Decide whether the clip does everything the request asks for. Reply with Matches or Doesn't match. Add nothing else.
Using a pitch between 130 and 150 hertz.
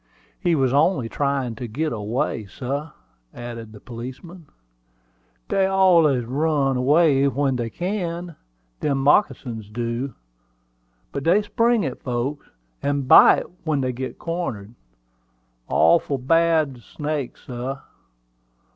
Matches